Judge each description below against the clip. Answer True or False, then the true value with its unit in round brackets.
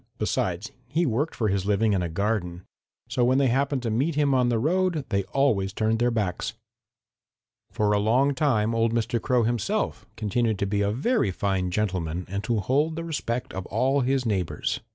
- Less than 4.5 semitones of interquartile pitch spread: False (4.8 semitones)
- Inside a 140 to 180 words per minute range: False (195 wpm)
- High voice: False (115 Hz)